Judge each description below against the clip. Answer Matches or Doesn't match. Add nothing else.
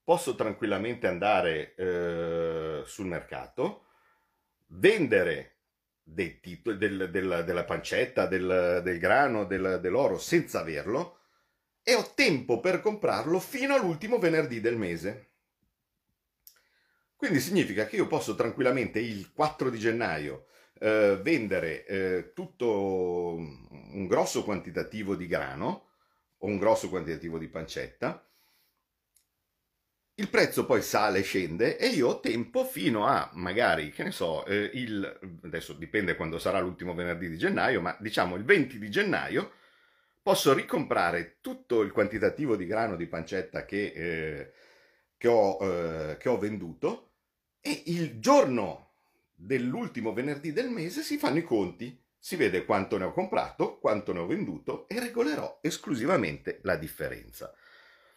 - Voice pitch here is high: Doesn't match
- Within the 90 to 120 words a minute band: Doesn't match